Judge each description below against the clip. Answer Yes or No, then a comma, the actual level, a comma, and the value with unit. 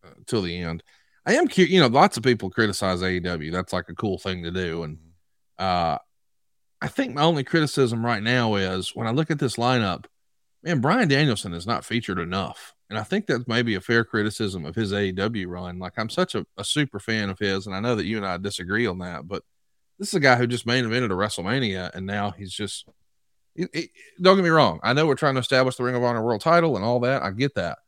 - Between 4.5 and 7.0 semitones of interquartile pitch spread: Yes, average, 5.2 semitones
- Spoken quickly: Yes, fast, 245 wpm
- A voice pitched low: Yes, low, 110 Hz